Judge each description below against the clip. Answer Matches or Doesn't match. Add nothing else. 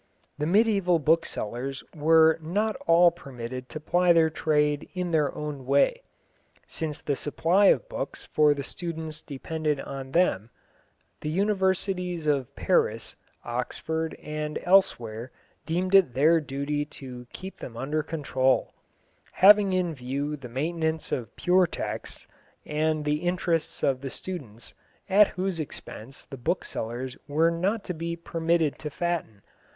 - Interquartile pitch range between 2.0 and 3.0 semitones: Doesn't match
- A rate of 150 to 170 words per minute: Doesn't match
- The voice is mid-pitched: Matches